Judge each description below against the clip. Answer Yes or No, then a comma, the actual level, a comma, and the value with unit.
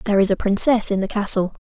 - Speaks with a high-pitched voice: Yes, high, 205 Hz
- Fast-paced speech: Yes, fast, 260 wpm